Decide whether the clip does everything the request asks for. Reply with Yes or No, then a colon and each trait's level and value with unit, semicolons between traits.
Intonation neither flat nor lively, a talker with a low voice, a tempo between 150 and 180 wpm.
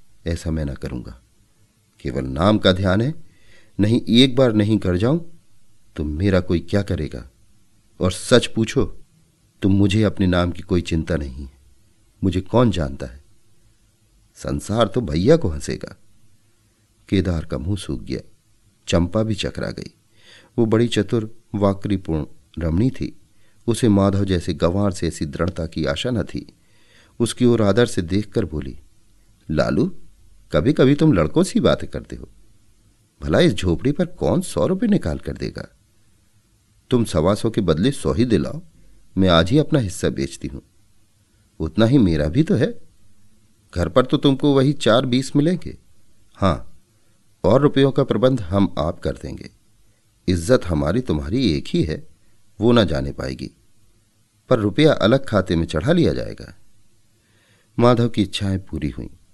Yes: average, 3.8 semitones; low, 105 Hz; average, 155 wpm